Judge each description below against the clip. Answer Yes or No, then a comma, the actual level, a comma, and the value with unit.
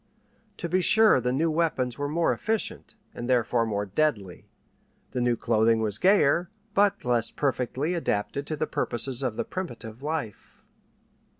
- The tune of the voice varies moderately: No, wide, 6.1 semitones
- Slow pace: No, average, 145 wpm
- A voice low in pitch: Yes, low, 130 Hz